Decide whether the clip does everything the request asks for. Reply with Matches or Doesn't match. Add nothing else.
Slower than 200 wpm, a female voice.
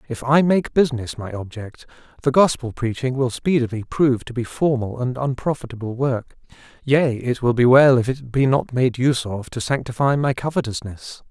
Doesn't match